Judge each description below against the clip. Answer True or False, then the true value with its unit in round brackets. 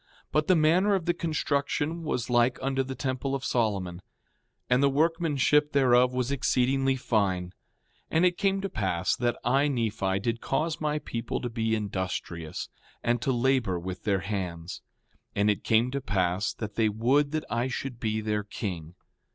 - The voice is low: True (120 Hz)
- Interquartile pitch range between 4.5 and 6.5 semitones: True (5.3 semitones)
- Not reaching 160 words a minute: False (175 wpm)